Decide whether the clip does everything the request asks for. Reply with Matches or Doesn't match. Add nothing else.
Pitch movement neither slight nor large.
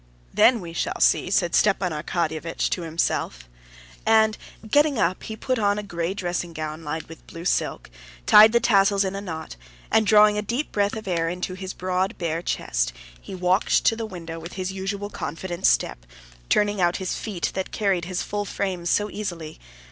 Matches